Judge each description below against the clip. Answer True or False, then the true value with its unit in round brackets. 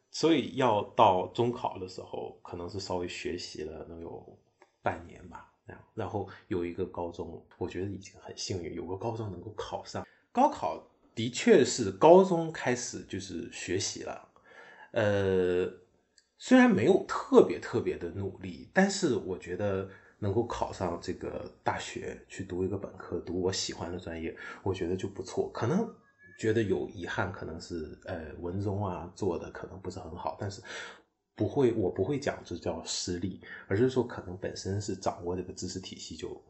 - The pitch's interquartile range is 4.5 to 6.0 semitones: False (3.7 semitones)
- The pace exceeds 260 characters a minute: False (255 characters per minute)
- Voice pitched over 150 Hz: False (95 Hz)